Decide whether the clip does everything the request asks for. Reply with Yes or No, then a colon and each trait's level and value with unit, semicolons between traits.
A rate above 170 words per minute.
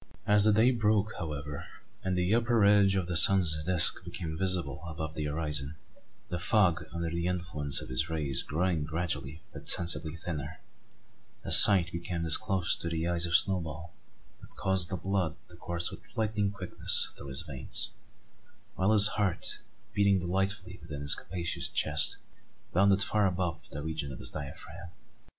No: average, 165 wpm